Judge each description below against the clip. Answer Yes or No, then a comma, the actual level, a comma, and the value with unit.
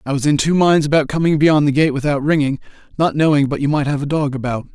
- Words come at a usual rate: No, fast, 265 wpm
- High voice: No, medium, 145 Hz